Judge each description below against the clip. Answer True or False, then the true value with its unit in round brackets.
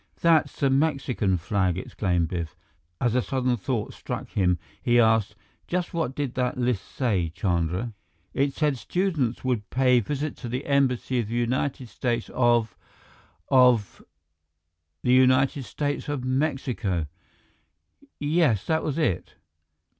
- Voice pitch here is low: True (125 Hz)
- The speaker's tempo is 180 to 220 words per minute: False (140 wpm)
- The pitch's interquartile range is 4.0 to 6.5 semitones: True (5.1 semitones)